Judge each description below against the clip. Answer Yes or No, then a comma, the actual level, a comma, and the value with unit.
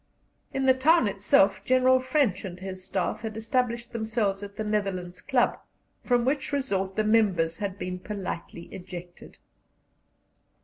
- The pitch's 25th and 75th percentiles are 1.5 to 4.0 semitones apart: No, average, 4.8 semitones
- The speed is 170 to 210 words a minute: No, average, 140 wpm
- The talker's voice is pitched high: Yes, high, 210 Hz